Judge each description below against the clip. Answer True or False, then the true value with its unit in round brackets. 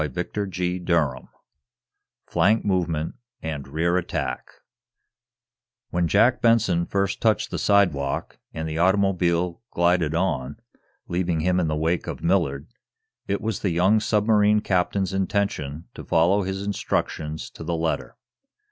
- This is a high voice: False (90 Hz)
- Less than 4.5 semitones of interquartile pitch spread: True (3.5 semitones)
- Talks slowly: True (130 wpm)